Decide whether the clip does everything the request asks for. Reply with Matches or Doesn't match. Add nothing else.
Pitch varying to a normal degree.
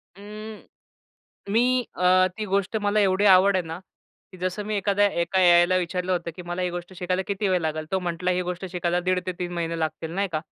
Doesn't match